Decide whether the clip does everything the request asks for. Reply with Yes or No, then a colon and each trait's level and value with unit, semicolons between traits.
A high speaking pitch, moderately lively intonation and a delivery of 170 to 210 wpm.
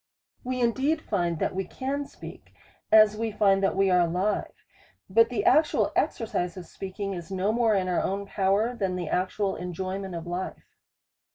Yes: high, 195 Hz; average, 3.5 semitones; average, 175 wpm